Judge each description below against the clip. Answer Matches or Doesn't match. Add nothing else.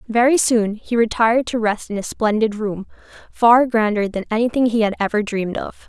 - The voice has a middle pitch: Doesn't match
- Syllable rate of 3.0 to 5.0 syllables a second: Doesn't match